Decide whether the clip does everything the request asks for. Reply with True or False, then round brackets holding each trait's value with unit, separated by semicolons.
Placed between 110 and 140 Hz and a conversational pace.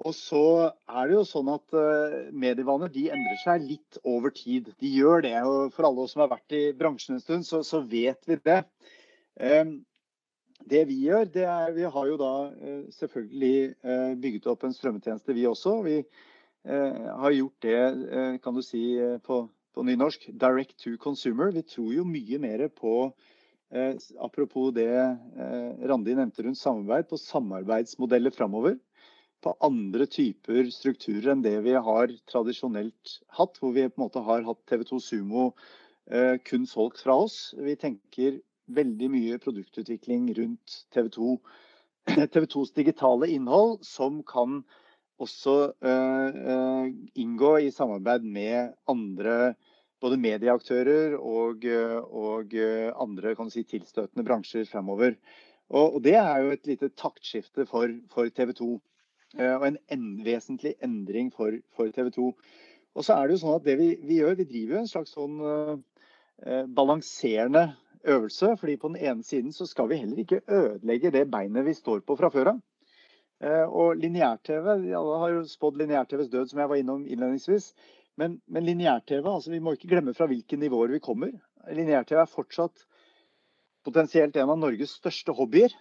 True (135 Hz; 160 wpm)